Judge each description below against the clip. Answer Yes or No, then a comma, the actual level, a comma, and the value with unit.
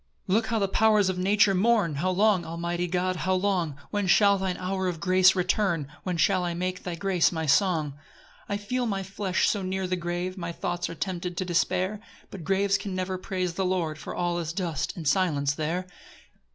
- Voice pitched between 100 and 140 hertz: No, medium, 185 Hz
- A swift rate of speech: Yes, fast, 210 wpm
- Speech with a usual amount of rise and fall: No, narrow, 2.1 semitones